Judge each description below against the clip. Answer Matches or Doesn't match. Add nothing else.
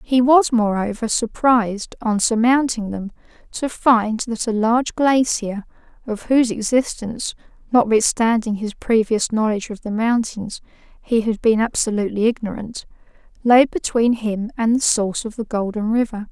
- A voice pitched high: Matches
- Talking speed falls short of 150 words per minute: Matches